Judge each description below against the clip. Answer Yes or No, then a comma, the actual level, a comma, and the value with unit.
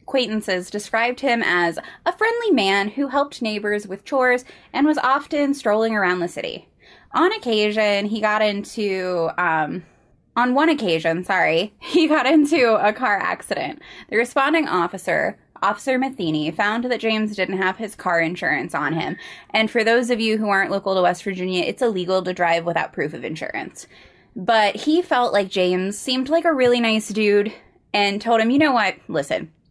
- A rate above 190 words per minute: No, average, 175 wpm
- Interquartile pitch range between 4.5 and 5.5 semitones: Yes, average, 5.0 semitones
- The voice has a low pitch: No, high, 215 Hz